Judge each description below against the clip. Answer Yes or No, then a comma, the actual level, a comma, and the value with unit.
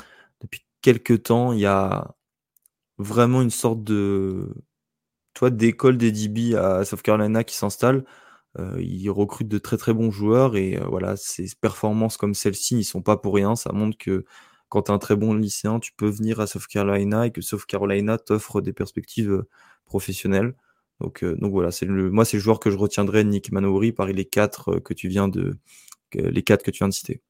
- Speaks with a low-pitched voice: Yes, low, 105 Hz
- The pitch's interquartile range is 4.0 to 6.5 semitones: No, narrow, 2.5 semitones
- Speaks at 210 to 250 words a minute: No, average, 195 wpm